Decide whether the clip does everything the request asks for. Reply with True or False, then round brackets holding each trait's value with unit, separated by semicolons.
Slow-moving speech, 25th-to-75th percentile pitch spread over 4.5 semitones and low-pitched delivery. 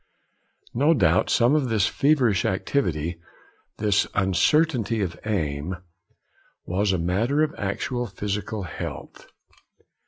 True (105 wpm; 5.2 semitones; 105 Hz)